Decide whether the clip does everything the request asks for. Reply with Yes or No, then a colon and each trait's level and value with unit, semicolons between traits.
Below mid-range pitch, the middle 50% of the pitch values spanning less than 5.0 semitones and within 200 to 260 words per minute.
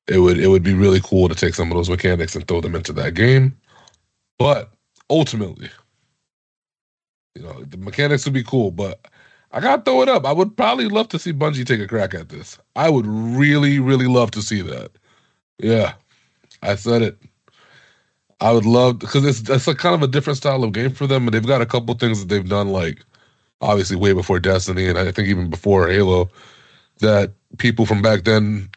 No: low, 110 Hz; wide, 5.5 semitones; fast, 205 wpm